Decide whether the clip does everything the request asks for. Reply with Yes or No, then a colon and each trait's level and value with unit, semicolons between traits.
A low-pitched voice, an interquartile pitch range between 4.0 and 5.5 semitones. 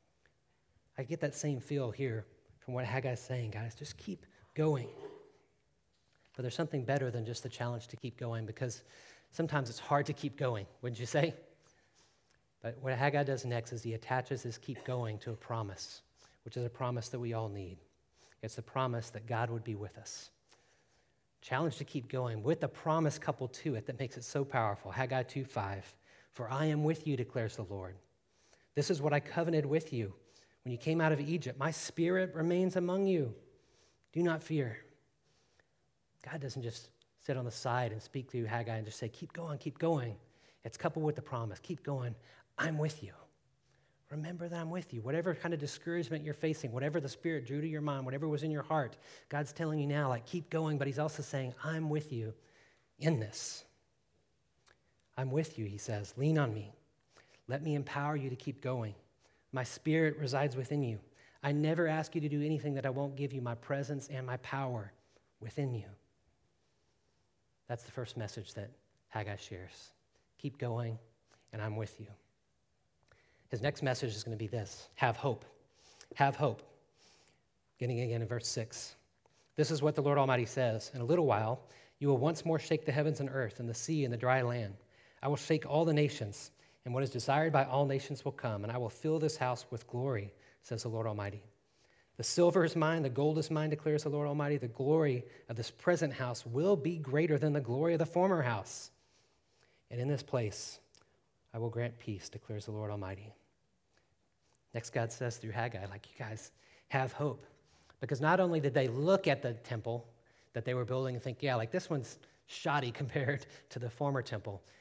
Yes: low, 130 Hz; average, 4.3 semitones